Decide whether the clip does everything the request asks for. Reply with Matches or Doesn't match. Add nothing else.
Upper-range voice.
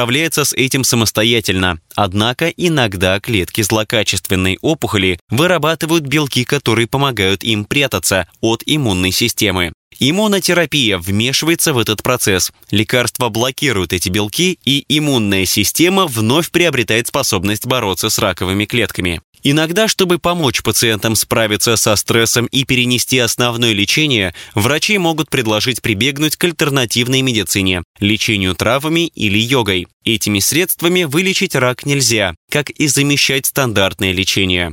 Doesn't match